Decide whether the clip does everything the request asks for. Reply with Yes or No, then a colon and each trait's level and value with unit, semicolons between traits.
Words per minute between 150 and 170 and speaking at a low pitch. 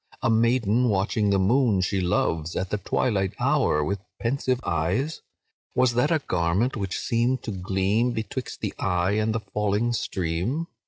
Yes: average, 160 wpm; low, 105 Hz